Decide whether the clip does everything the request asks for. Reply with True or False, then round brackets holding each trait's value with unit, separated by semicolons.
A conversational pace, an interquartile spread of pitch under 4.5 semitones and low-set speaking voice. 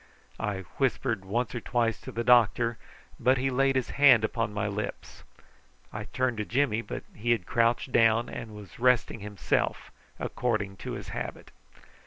True (165 wpm; 2.8 semitones; 115 Hz)